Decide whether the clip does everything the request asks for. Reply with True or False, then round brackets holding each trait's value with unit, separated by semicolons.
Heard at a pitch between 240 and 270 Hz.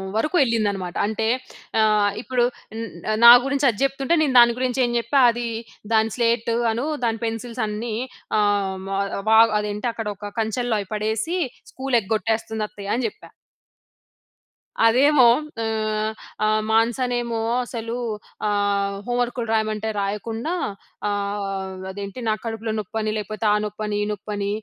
False (220 Hz)